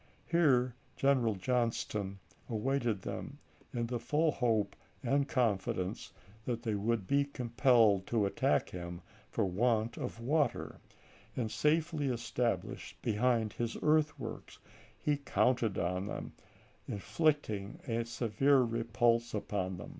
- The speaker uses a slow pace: Yes, slow, 115 wpm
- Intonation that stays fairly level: No, average, 4.0 semitones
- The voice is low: Yes, low, 120 Hz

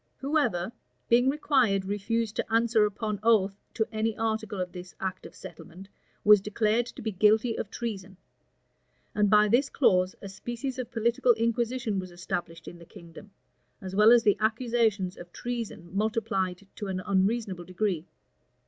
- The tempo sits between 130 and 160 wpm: Yes, average, 155 wpm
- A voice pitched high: Yes, high, 210 Hz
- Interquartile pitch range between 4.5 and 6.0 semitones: No, average, 3.5 semitones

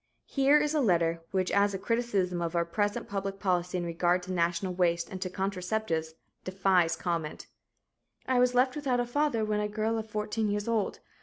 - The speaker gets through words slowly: No, average, 190 wpm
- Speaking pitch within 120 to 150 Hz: No, high, 195 Hz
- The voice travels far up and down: No, average, 3.9 semitones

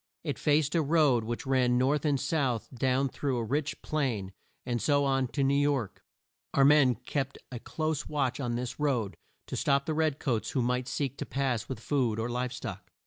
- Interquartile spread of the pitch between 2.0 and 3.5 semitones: Yes, average, 2.8 semitones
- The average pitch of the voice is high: No, low, 135 Hz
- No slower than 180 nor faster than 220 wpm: Yes, average, 200 wpm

